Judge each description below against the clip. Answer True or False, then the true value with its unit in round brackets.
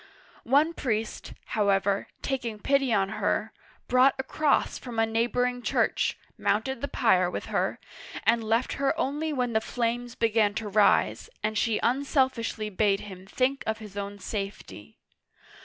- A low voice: False (225 Hz)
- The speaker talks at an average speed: True (155 wpm)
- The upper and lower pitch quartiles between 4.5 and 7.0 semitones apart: False (3.5 semitones)